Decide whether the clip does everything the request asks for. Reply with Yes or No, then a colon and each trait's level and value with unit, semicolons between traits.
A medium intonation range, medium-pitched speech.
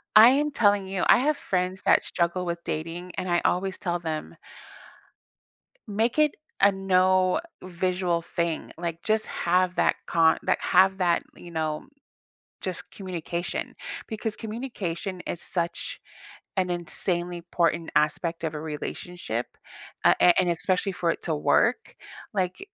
No: narrow, 2.2 semitones; medium, 180 Hz